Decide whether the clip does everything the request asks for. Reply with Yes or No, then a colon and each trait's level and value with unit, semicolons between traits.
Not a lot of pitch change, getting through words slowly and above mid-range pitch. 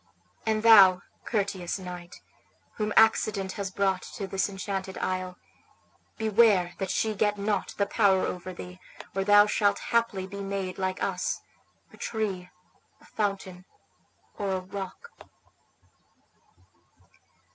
Yes: narrow, 1.9 semitones; slow, 125 wpm; high, 195 Hz